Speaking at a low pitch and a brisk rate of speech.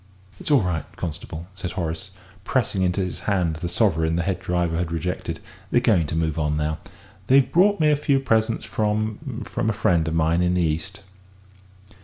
No: very low, 90 Hz; average, 190 wpm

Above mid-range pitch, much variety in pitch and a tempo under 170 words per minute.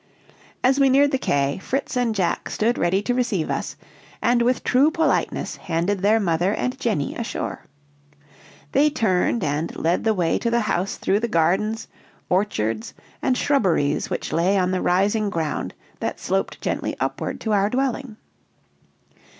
Yes: high, 210 Hz; wide, 5.8 semitones; average, 160 wpm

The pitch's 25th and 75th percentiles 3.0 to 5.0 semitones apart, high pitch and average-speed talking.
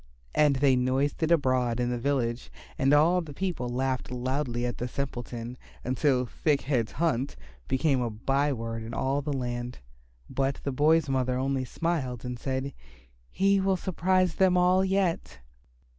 No: average, 4.0 semitones; low, 135 Hz; average, 160 wpm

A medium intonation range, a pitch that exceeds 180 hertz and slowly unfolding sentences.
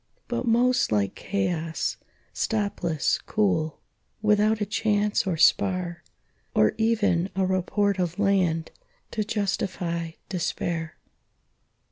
Yes: average, 3.6 semitones; high, 190 Hz; slow, 100 wpm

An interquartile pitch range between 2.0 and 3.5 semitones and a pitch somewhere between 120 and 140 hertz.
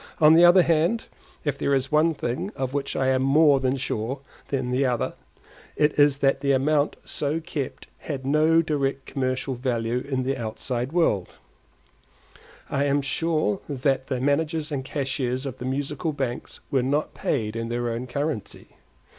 Yes: average, 2.8 semitones; low, 135 Hz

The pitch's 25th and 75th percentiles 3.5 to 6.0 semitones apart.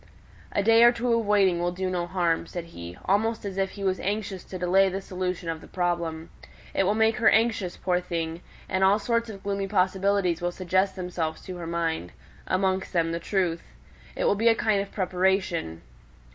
No: narrow, 2.5 semitones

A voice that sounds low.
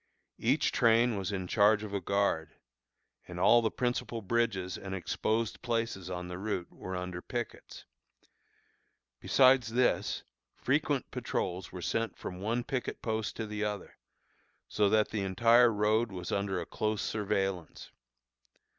Yes: low, 105 Hz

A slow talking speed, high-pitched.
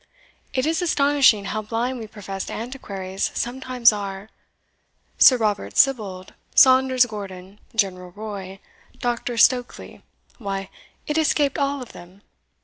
Yes: slow, 120 wpm; high, 220 Hz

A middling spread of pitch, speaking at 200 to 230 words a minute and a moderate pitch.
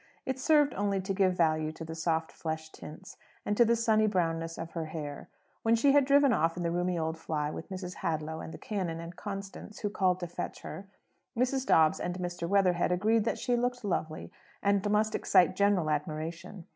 Yes: average, 4.4 semitones; fast, 205 wpm; medium, 180 Hz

